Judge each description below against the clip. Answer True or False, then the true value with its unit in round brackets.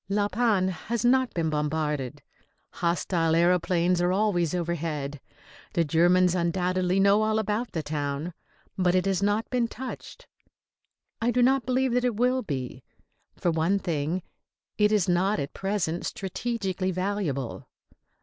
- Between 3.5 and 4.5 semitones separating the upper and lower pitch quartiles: True (4.2 semitones)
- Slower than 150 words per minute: True (140 wpm)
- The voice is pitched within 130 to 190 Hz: True (185 Hz)